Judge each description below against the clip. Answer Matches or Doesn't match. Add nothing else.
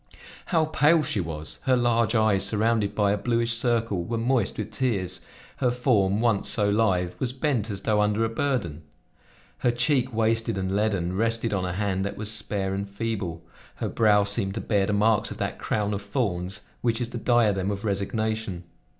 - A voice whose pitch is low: Matches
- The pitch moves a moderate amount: Matches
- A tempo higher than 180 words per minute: Matches